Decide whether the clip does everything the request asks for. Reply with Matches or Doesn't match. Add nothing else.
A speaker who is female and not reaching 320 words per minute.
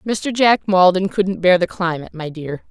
Matches